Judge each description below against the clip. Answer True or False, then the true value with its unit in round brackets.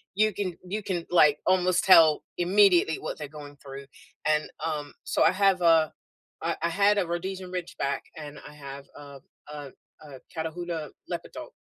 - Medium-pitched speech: True (165 Hz)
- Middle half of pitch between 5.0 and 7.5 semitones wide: False (3.8 semitones)